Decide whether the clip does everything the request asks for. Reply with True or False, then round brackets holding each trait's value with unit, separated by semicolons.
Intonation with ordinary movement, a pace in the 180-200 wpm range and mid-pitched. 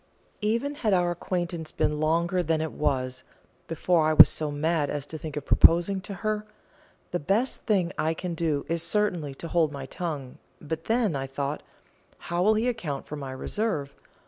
True (3.9 semitones; 185 wpm; 165 Hz)